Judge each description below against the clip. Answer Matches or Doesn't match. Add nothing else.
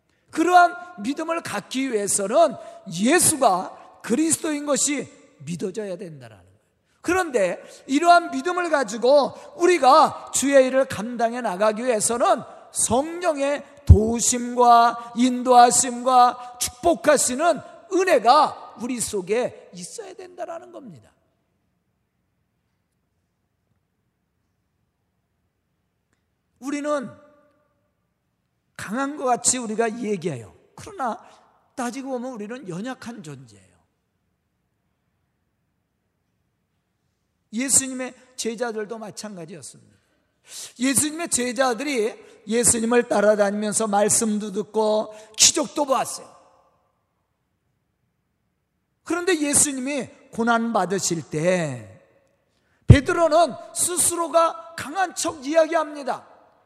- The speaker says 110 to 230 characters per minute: Matches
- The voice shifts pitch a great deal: Matches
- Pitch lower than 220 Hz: Doesn't match